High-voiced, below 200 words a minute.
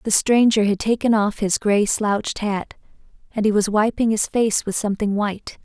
Yes: high, 210 Hz; average, 190 wpm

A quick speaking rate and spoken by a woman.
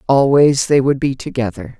No: average, 165 wpm; female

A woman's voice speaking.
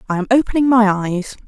Yes: female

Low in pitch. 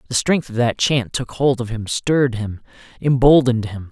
Yes: low, 125 Hz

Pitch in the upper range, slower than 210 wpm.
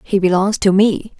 Yes: high, 195 Hz; average, 200 wpm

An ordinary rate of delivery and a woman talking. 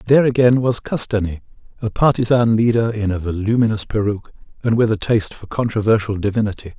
No: average, 160 wpm; male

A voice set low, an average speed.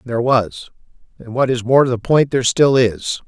No: low, 125 Hz; fast, 220 wpm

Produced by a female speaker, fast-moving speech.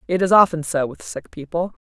Yes: female; fast, 230 wpm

